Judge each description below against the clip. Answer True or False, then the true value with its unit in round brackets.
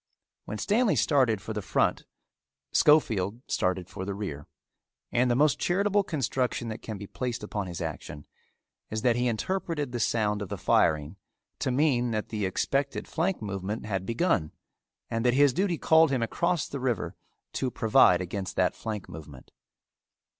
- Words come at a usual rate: True (165 wpm)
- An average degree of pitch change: False (6.0 semitones)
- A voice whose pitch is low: True (115 Hz)